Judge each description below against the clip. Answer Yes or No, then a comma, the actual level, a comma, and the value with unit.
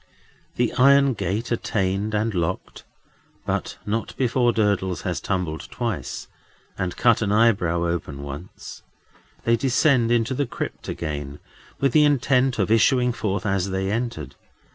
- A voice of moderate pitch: No, low, 110 Hz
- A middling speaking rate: No, slow, 130 wpm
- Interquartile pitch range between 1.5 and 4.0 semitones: No, average, 4.8 semitones